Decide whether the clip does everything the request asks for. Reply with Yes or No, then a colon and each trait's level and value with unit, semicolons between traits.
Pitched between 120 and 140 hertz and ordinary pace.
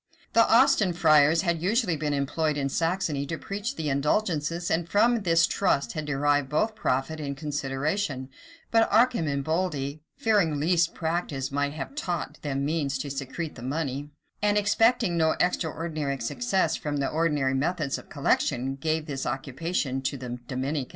No: medium, 155 Hz; average, 155 wpm